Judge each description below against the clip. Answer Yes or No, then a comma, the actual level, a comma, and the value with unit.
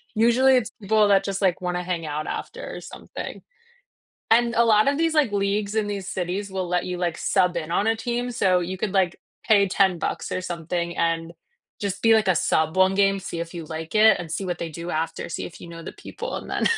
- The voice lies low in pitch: No, high, 190 Hz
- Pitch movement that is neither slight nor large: Yes, average, 3.7 semitones